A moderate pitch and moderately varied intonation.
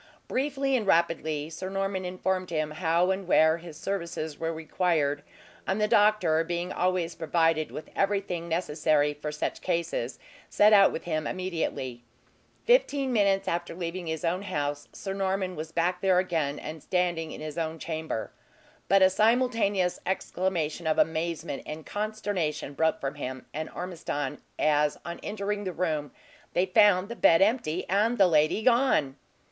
Yes: medium, 175 Hz; average, 3.6 semitones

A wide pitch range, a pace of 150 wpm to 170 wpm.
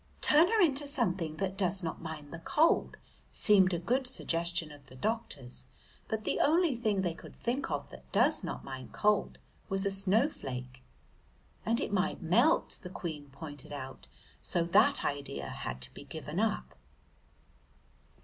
Yes: wide, 7.5 semitones; average, 160 wpm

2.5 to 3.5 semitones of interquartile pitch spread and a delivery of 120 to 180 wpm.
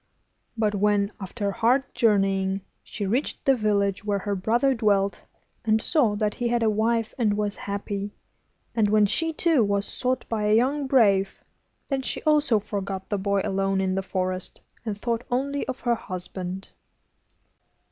Yes: average, 3.1 semitones; average, 165 wpm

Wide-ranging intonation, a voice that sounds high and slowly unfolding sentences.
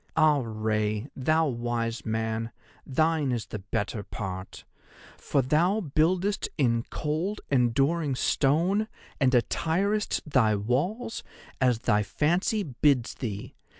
No: wide, 6.2 semitones; low, 135 Hz; slow, 115 wpm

